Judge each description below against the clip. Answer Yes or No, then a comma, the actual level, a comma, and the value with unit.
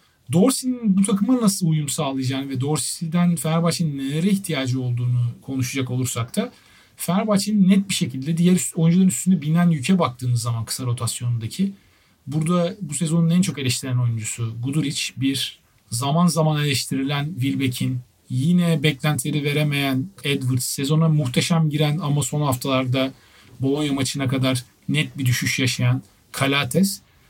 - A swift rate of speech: No, average, 130 wpm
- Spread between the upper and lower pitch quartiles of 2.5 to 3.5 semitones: No, average, 4.6 semitones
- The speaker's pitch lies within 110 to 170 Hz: Yes, medium, 140 Hz